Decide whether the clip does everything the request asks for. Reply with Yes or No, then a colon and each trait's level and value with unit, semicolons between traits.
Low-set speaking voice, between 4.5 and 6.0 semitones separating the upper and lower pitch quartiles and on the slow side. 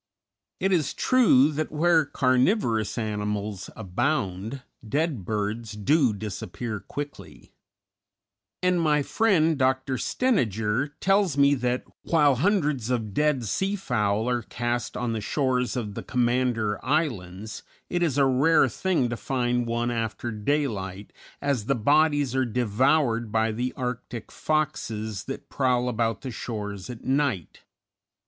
Yes: low, 125 Hz; average, 4.9 semitones; slow, 130 wpm